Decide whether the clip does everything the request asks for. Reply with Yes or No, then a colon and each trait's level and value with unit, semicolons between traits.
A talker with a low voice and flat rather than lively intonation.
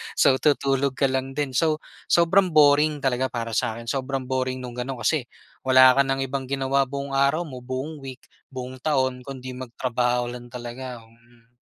Yes: low, 130 Hz; narrow, 1.8 semitones